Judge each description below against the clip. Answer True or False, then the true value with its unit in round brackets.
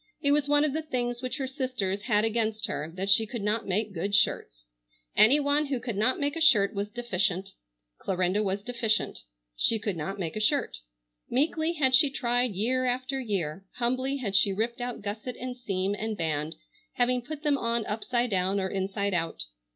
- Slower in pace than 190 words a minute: False (195 wpm)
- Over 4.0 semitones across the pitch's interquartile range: True (4.5 semitones)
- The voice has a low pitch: False (225 Hz)